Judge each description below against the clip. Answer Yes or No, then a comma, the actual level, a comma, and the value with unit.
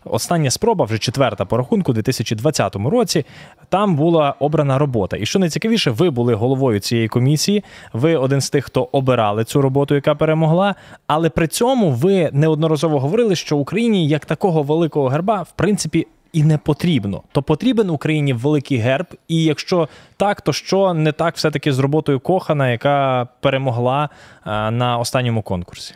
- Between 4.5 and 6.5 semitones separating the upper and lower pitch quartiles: No, average, 4.1 semitones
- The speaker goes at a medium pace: No, fast, 160 wpm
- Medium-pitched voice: Yes, medium, 150 Hz